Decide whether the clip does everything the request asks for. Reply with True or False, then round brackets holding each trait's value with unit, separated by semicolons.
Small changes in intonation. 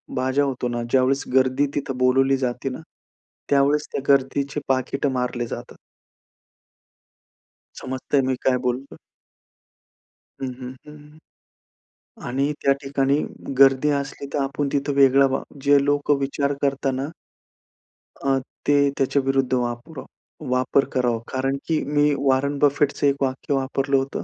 True (1.3 semitones)